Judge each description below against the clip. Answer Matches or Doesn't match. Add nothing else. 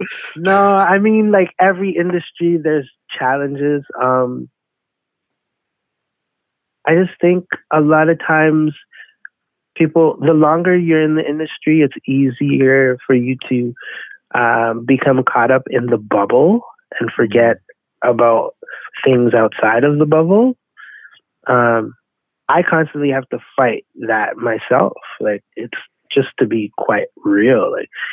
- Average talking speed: Doesn't match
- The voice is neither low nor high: Matches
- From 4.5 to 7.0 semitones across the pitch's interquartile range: Matches